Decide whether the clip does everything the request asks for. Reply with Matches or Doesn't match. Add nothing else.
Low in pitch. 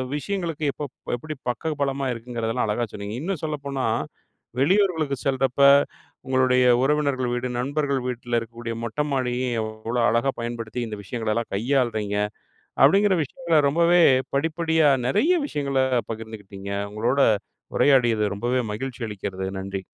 Matches